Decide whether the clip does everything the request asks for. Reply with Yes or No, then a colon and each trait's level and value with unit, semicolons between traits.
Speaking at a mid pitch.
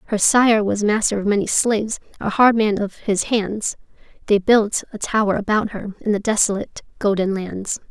No: high, 210 Hz